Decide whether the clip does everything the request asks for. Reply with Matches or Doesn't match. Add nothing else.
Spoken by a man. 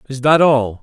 Matches